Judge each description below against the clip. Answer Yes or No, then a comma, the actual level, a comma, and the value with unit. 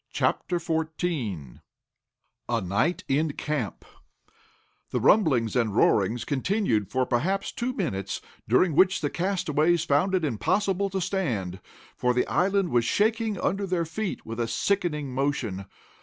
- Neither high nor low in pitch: Yes, medium, 155 Hz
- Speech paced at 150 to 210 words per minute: No, average, 140 wpm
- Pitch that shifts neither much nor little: No, wide, 7.8 semitones